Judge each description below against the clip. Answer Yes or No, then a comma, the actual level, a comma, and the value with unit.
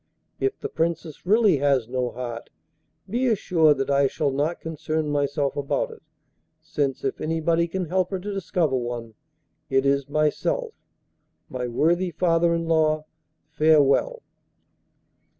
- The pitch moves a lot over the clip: No, average, 3.9 semitones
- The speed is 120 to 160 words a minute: Yes, slow, 135 wpm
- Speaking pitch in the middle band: Yes, medium, 155 Hz